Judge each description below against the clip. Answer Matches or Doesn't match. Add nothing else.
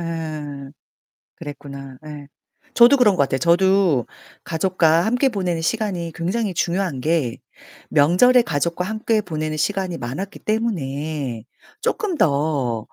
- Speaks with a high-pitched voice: Doesn't match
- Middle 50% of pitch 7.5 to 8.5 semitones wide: Doesn't match